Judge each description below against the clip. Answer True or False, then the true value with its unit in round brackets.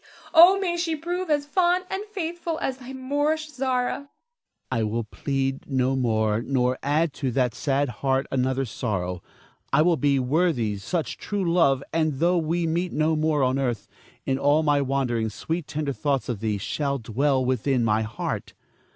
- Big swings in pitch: True (7.4 semitones)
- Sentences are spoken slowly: False (175 wpm)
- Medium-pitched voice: True (145 Hz)